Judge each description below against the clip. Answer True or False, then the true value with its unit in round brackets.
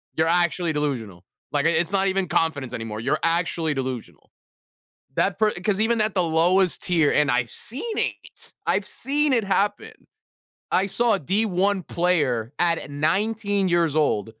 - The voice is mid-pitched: True (175 Hz)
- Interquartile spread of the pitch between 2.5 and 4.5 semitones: False (5.2 semitones)